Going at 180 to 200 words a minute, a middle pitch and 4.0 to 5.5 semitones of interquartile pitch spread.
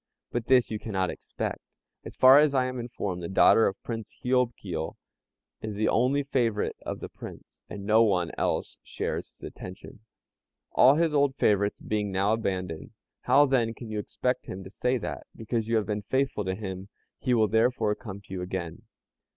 No: average, 190 wpm; low, 110 Hz; average, 4.3 semitones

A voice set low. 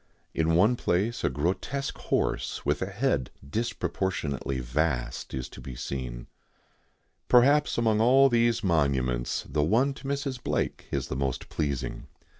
Yes: very low, 85 Hz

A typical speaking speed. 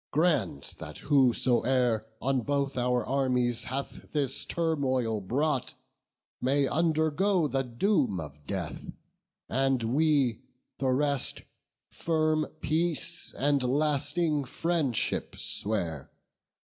No: slow, 95 wpm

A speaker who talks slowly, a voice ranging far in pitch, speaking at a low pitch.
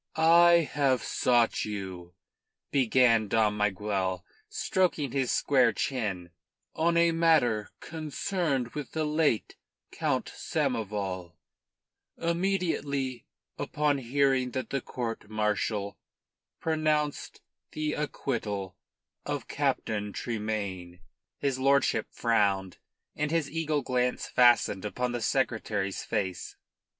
Yes: slow, 100 wpm; wide, 6.3 semitones; low, 125 Hz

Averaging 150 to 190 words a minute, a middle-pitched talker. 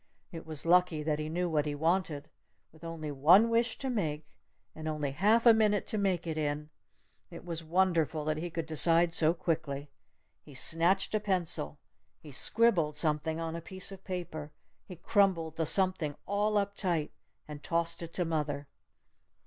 Yes: average, 175 wpm; medium, 165 Hz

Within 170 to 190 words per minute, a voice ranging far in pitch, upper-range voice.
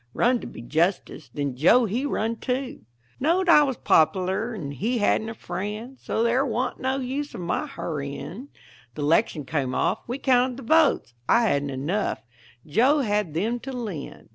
Yes: average, 175 wpm; wide, 7.5 semitones; high, 225 Hz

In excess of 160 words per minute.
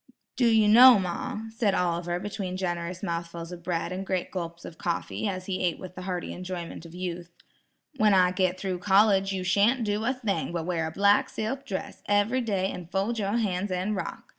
Yes: fast, 205 wpm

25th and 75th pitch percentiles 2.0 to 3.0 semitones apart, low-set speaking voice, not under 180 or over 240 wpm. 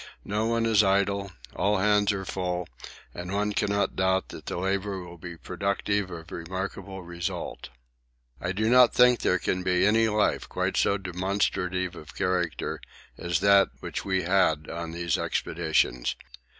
No: narrow, 2.4 semitones; very low, 95 Hz; average, 155 wpm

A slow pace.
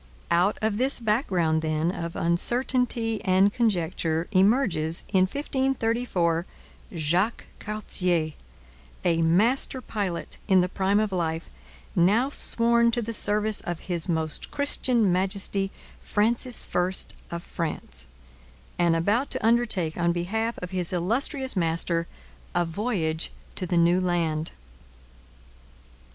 Yes: slow, 120 wpm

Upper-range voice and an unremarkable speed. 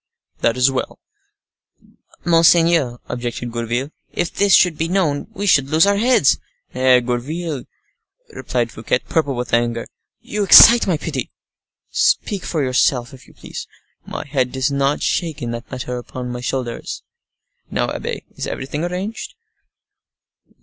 No: low, 135 Hz; average, 145 wpm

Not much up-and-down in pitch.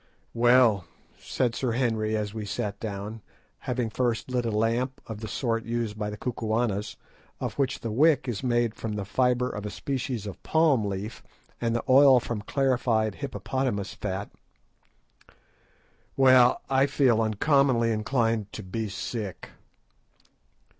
No: average, 3.1 semitones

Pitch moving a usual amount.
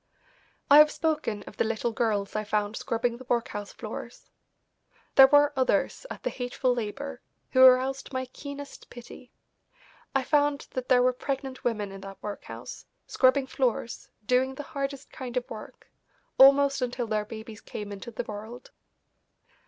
Yes: average, 3.7 semitones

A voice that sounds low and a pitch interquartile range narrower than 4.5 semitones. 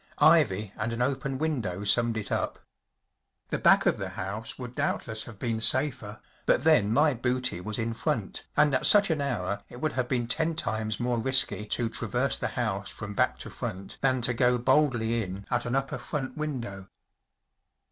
Yes: low, 120 Hz; average, 3.5 semitones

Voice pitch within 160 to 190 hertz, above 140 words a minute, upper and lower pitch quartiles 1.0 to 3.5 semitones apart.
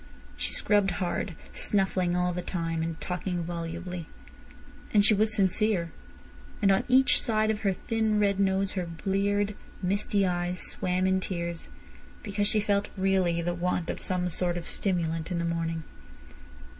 Yes: medium, 185 Hz; average, 155 wpm; average, 2.7 semitones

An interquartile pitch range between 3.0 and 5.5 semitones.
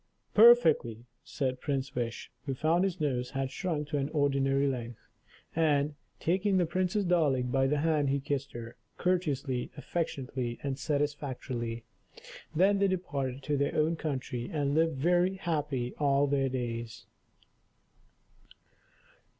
Yes: average, 3.8 semitones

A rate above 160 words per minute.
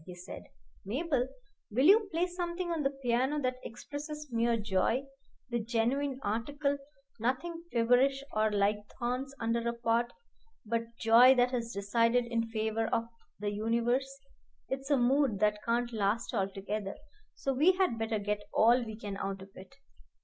No: average, 155 wpm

